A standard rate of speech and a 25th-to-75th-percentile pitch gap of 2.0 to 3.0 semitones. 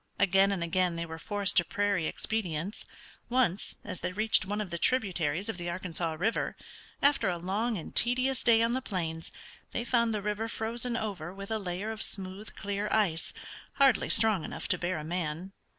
No: average, 190 wpm; average, 4.3 semitones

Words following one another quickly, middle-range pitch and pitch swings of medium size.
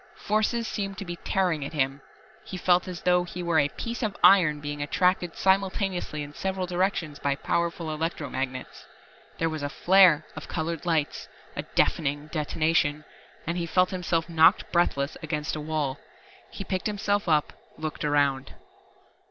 No: average, 160 wpm; medium, 165 Hz; average, 3.7 semitones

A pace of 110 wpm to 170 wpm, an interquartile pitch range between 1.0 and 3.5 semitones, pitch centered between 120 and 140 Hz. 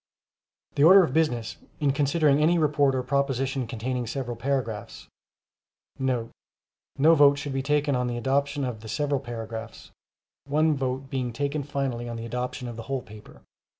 Yes: average, 155 wpm; average, 2.9 semitones; low, 135 Hz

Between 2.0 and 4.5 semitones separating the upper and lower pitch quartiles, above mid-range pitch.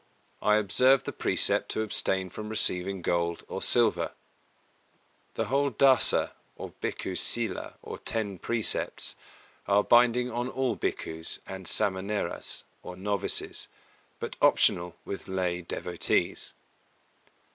No: average, 4.2 semitones; low, 100 Hz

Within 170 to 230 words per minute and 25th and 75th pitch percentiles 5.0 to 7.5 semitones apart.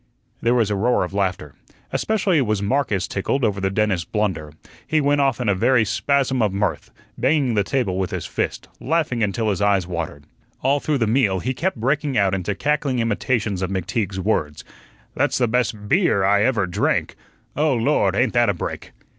Yes: average, 190 wpm; average, 5.3 semitones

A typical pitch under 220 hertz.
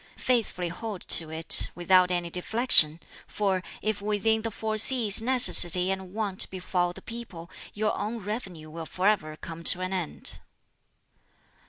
Yes: high, 190 Hz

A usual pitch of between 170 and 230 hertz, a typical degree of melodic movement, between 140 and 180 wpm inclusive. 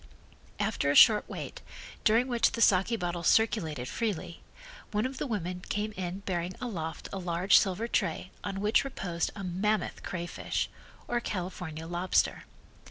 Yes: high, 190 Hz; average, 3.7 semitones; average, 150 wpm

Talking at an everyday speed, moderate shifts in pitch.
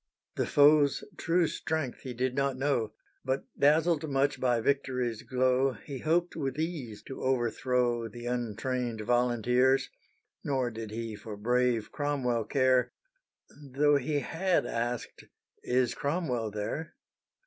No: slow, 125 wpm; average, 3.1 semitones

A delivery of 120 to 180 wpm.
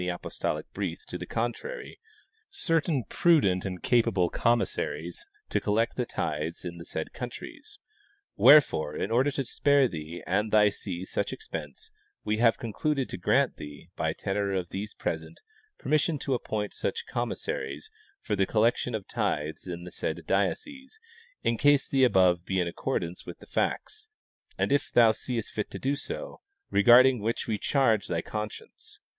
Yes: average, 165 wpm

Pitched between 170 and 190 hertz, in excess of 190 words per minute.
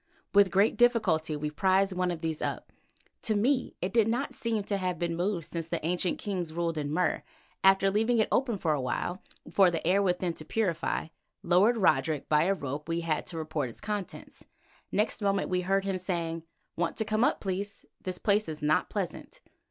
Yes: medium, 185 Hz; fast, 205 wpm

